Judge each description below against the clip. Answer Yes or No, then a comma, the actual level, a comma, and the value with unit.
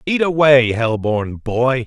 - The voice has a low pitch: Yes, low, 125 Hz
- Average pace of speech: Yes, average, 160 wpm